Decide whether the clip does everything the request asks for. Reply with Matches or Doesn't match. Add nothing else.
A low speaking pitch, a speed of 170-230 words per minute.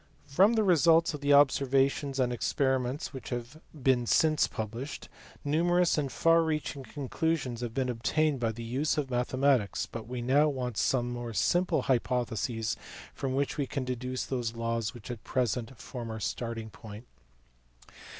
Doesn't match